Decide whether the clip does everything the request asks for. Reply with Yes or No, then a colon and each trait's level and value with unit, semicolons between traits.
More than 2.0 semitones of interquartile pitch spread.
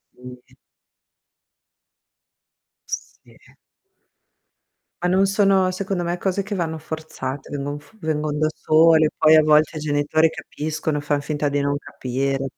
Yes: average, 2.7 semitones